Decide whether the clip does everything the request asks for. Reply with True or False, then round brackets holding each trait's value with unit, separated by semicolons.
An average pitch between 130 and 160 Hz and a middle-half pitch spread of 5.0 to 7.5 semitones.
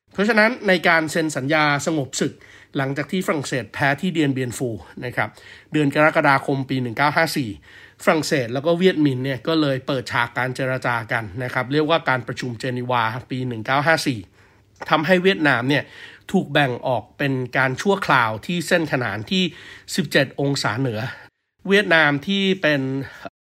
False (140 Hz; 4.1 semitones)